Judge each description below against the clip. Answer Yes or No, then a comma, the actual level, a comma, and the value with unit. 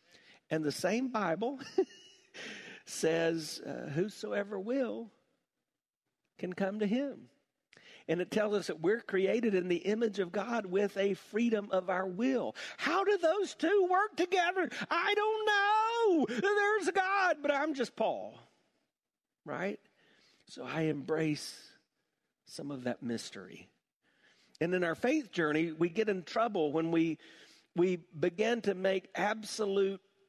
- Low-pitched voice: No, high, 210 Hz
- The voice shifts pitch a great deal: Yes, wide, 8.4 semitones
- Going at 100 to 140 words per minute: Yes, slow, 135 wpm